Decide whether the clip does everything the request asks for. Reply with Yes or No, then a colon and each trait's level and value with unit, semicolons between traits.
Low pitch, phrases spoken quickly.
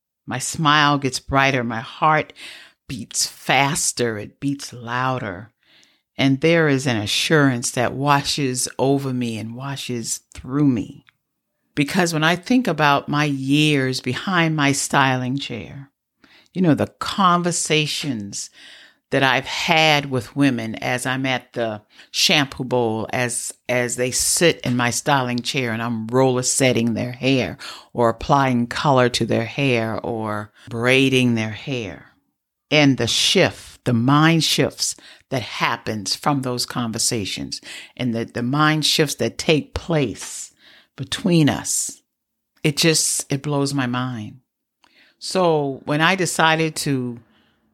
No: low, 130 Hz; slow, 135 wpm